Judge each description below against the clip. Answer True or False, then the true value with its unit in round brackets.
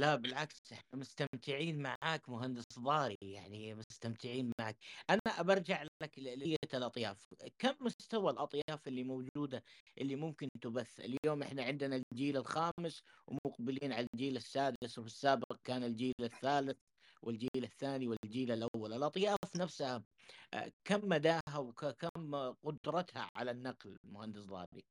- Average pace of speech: True (125 wpm)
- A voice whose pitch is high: False (135 Hz)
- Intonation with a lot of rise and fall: False (3.7 semitones)